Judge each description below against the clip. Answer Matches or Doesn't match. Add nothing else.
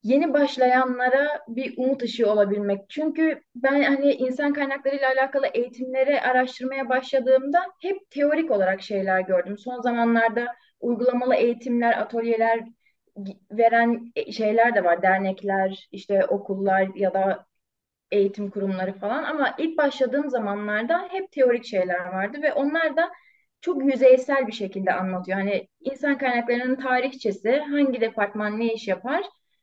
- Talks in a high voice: Matches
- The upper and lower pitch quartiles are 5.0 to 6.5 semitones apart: Matches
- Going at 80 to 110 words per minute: Doesn't match